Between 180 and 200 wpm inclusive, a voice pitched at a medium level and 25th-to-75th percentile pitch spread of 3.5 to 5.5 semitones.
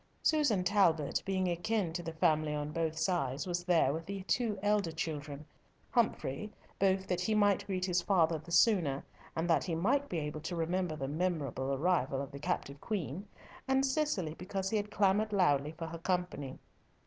Yes: average, 185 wpm; medium, 175 Hz; average, 4.1 semitones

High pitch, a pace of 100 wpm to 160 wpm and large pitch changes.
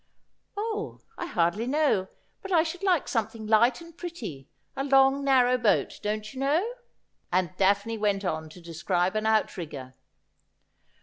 Yes: high, 225 Hz; average, 150 wpm; wide, 7.3 semitones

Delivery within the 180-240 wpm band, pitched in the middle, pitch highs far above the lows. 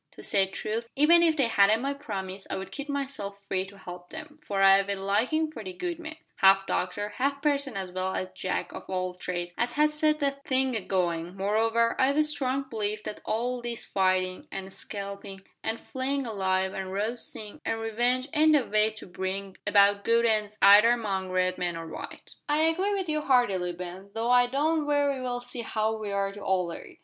No: average, 200 wpm; high, 215 Hz; wide, 5.9 semitones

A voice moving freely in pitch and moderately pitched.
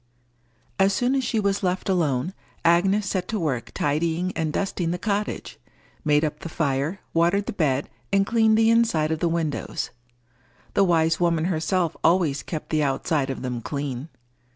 No: average, 4.4 semitones; medium, 170 Hz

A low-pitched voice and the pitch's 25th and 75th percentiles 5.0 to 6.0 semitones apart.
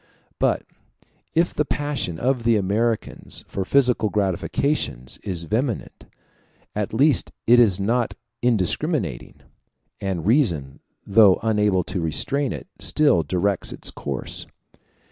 Yes: low, 105 Hz; average, 5.3 semitones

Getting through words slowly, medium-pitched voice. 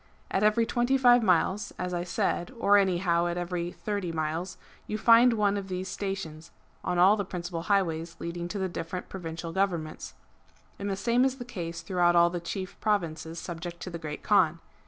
No: average, 195 wpm; medium, 180 Hz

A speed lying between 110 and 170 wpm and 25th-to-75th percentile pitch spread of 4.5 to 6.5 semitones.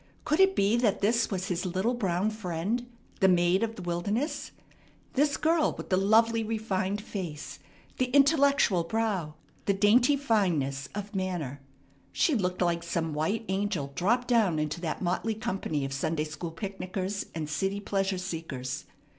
Yes: average, 155 wpm; average, 4.8 semitones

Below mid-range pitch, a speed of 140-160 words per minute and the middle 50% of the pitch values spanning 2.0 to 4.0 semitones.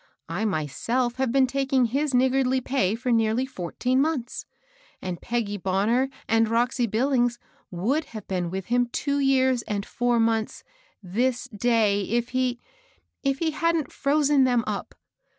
No: high, 245 Hz; average, 150 wpm; average, 3.4 semitones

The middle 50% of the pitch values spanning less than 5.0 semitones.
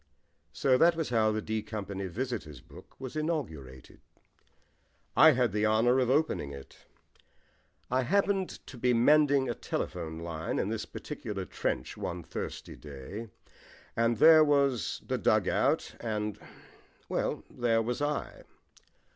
No: average, 5.3 semitones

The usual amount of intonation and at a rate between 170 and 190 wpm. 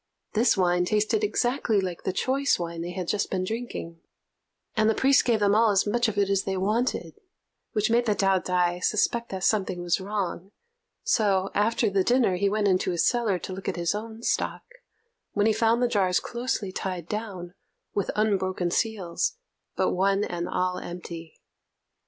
Yes: average, 3.3 semitones; average, 180 wpm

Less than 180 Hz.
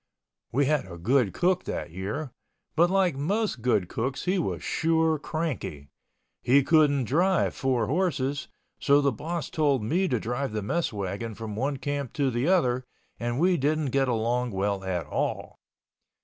Yes: low, 135 Hz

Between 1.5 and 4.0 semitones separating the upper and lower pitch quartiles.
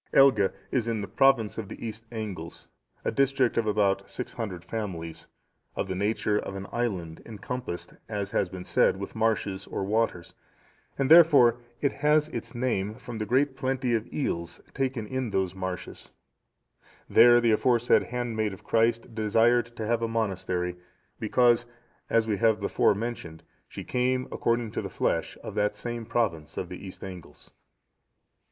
Yes: average, 3.7 semitones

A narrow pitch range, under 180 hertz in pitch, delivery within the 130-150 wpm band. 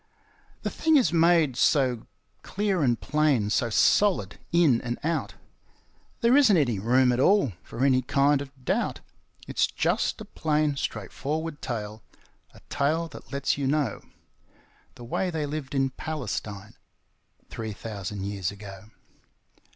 No: wide, 5.5 semitones; low, 135 Hz; average, 140 wpm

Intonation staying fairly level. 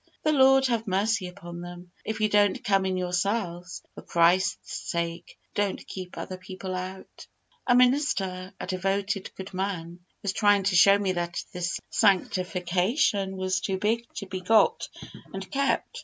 Yes: narrow, 2.2 semitones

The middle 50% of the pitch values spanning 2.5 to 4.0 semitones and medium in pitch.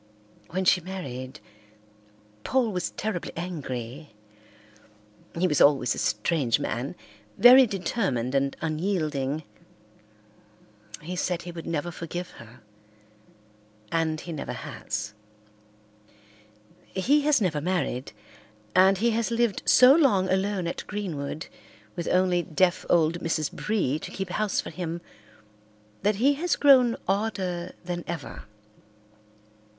No: average, 4.6 semitones; medium, 175 Hz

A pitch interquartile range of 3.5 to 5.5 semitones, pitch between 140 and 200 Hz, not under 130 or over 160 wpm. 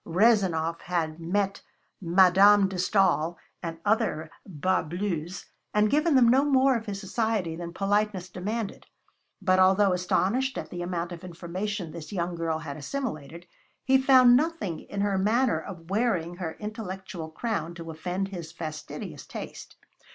Yes: average, 4.0 semitones; medium, 185 Hz; average, 150 wpm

